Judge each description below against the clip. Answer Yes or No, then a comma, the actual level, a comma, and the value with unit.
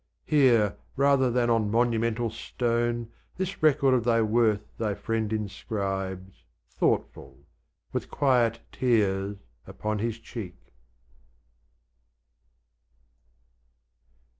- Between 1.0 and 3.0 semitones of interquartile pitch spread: Yes, narrow, 2.5 semitones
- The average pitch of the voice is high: No, low, 115 Hz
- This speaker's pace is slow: Yes, slow, 90 wpm